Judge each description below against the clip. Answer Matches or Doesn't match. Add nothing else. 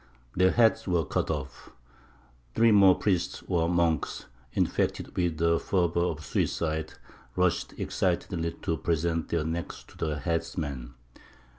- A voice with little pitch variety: Matches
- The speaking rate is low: Matches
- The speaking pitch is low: Matches